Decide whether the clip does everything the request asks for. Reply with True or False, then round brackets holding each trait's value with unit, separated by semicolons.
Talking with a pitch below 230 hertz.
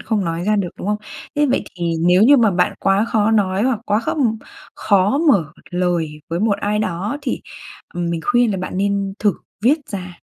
True (200 Hz)